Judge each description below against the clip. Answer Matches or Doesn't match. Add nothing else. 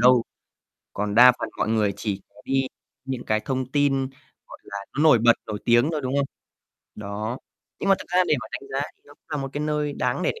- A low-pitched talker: Matches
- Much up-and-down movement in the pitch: Doesn't match